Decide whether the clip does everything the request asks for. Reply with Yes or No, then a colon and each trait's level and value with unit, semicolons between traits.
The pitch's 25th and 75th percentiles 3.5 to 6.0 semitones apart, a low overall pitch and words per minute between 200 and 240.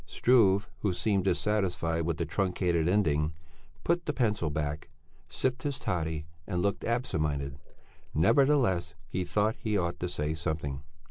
No: average, 5.0 semitones; very low, 90 Hz; average, 145 wpm